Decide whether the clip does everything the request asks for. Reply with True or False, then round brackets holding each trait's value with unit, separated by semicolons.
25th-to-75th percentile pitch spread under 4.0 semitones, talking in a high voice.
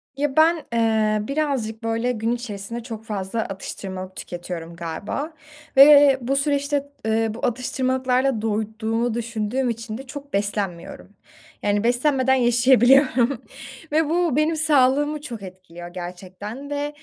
False (4.6 semitones; 235 Hz)